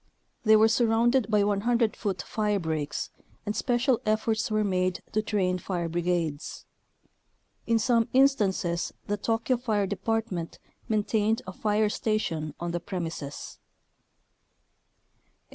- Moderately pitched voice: No, high, 210 Hz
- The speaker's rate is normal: No, slow, 115 wpm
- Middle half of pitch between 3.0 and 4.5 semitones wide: Yes, average, 3.8 semitones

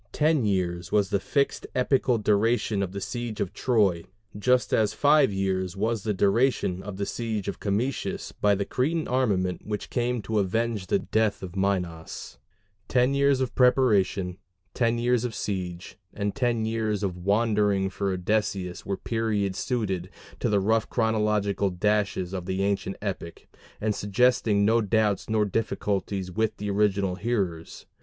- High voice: No, low, 105 Hz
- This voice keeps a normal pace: Yes, average, 155 wpm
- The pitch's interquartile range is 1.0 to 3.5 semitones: Yes, average, 3.1 semitones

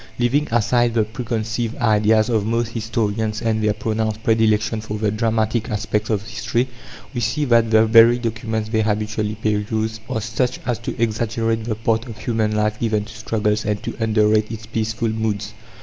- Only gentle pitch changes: Yes, narrow, 1.2 semitones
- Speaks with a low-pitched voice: Yes, low, 110 Hz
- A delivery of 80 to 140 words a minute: No, average, 175 wpm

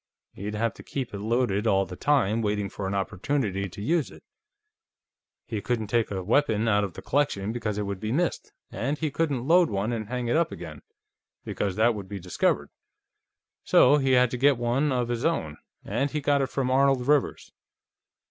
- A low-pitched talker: Yes, low, 120 Hz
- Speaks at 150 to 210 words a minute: Yes, average, 200 wpm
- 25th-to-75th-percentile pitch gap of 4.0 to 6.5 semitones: Yes, average, 5.0 semitones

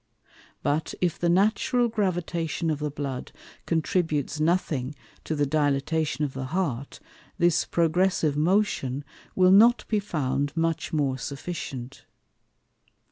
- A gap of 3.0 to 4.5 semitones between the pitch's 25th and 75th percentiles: Yes, average, 3.9 semitones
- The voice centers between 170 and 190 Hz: No, medium, 155 Hz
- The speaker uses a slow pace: Yes, slow, 120 wpm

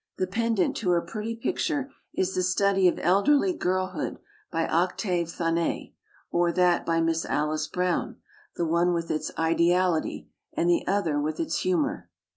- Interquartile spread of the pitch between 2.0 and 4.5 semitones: Yes, average, 3.1 semitones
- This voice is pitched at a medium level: Yes, medium, 180 Hz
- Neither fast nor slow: Yes, average, 155 wpm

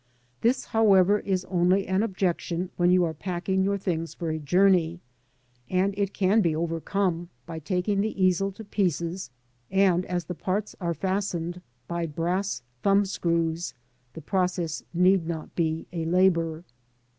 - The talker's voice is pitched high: No, medium, 180 Hz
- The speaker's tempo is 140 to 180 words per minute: Yes, average, 150 wpm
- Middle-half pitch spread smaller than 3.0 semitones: Yes, narrow, 2.5 semitones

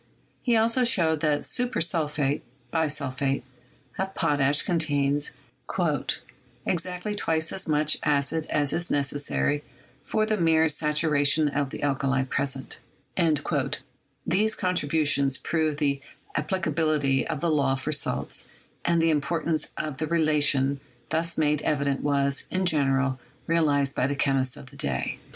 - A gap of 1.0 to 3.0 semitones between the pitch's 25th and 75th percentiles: Yes, average, 2.7 semitones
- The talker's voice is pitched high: No, medium, 150 Hz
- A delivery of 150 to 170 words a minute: No, slow, 135 wpm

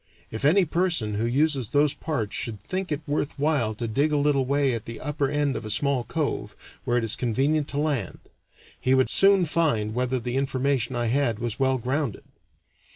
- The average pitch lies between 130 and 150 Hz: Yes, low, 135 Hz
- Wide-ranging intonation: No, average, 3.9 semitones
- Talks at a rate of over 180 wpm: Yes, average, 200 wpm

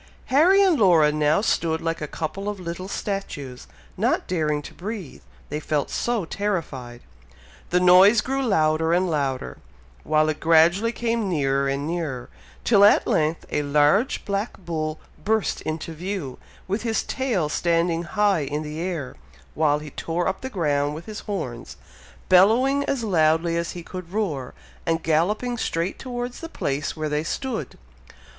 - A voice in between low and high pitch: Yes, medium, 170 Hz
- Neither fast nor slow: Yes, average, 160 wpm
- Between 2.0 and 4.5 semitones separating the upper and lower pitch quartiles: No, average, 5.1 semitones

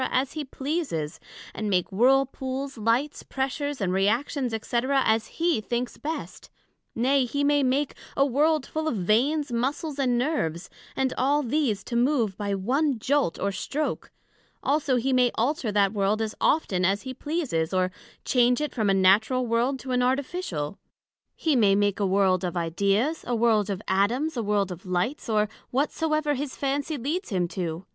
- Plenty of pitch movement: Yes, wide, 6.0 semitones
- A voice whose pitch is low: No, high, 245 Hz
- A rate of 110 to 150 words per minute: No, average, 175 wpm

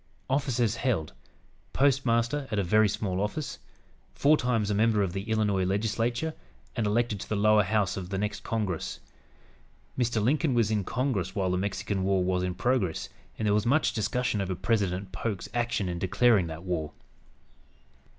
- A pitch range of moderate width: Yes, average, 3.8 semitones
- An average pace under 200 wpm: Yes, average, 170 wpm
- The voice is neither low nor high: No, low, 105 Hz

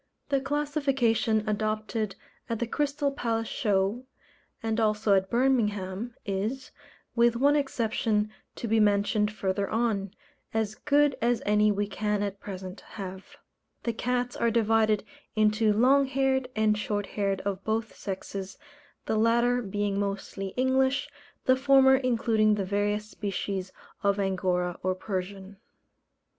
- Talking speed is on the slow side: Yes, slow, 130 wpm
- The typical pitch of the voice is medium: No, high, 215 Hz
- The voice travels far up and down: No, average, 3.3 semitones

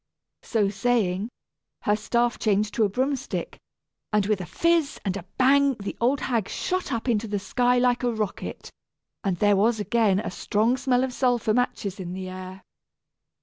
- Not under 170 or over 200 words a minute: Yes, average, 180 wpm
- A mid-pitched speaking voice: No, high, 220 Hz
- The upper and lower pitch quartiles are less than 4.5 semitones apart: Yes, average, 3.8 semitones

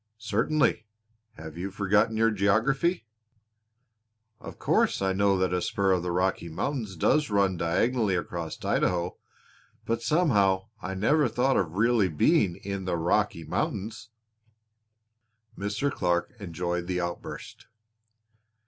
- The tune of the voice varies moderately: Yes, average, 4.0 semitones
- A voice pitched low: Yes, low, 100 Hz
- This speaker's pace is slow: Yes, slow, 125 wpm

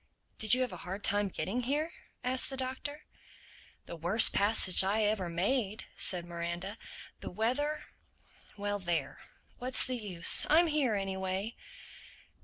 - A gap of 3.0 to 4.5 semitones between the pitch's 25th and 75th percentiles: No, average, 5.3 semitones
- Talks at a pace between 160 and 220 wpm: No, slow, 135 wpm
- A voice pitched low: No, high, 210 Hz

